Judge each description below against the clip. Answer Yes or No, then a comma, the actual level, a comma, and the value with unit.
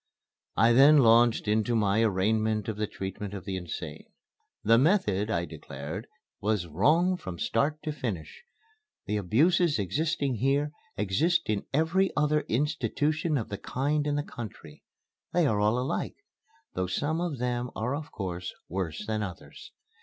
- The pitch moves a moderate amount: No, wide, 6.5 semitones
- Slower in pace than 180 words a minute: Yes, average, 155 wpm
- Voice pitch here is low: Yes, low, 115 Hz